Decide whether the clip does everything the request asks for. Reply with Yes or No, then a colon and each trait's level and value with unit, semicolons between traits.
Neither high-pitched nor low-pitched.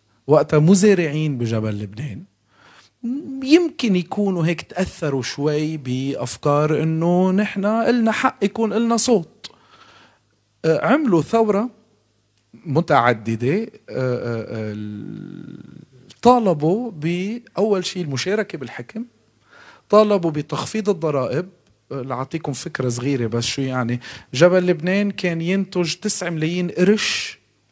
Yes: medium, 165 Hz